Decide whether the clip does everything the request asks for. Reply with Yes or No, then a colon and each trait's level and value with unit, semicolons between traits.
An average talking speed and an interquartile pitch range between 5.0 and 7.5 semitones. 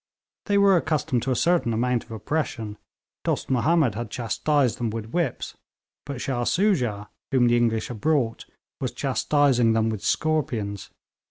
Yes: average, 155 wpm; average, 5.3 semitones